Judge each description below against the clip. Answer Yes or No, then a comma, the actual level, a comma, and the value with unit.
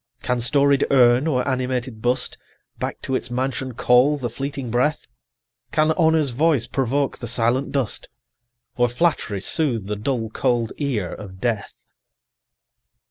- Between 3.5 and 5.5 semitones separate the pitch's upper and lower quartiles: No, average, 2.9 semitones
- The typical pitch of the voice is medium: No, low, 125 Hz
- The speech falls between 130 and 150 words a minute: Yes, average, 140 wpm